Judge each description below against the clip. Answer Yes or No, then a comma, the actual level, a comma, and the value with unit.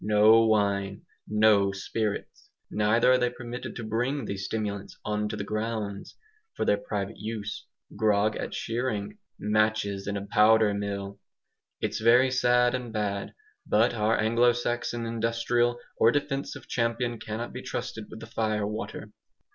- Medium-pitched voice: No, low, 110 Hz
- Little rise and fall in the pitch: Yes, narrow, 2.2 semitones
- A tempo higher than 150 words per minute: No, average, 145 wpm